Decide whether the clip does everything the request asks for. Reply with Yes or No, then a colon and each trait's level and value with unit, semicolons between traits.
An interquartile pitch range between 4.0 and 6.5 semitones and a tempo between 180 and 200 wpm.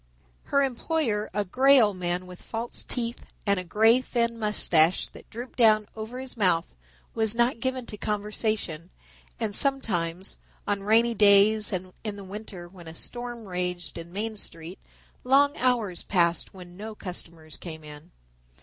No: average, 4.5 semitones; average, 160 wpm